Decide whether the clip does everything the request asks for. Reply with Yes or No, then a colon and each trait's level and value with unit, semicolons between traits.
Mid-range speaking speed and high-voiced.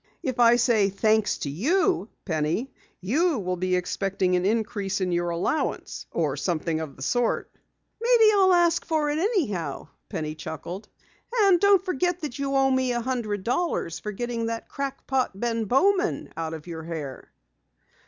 Yes: average, 165 wpm; high, 230 Hz